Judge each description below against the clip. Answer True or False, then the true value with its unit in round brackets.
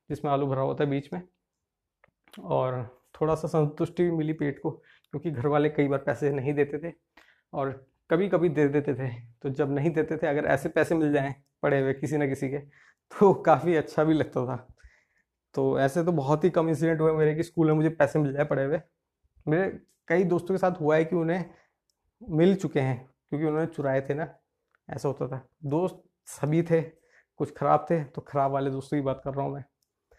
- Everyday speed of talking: False (210 wpm)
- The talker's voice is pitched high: False (150 Hz)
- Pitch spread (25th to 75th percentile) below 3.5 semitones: True (3.0 semitones)